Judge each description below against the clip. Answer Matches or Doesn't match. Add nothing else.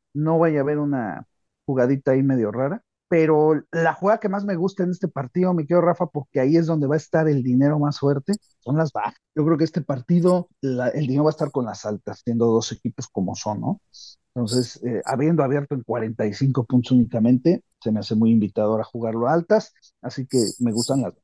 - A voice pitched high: Doesn't match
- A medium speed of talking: Doesn't match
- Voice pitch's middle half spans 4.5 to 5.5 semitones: Matches